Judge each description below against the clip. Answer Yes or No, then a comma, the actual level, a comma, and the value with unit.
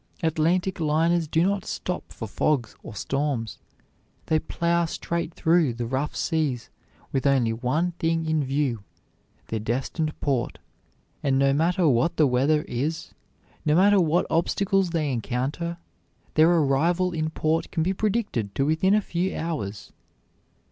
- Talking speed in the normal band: Yes, average, 145 wpm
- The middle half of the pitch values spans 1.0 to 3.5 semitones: No, average, 4.2 semitones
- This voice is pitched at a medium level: Yes, medium, 155 Hz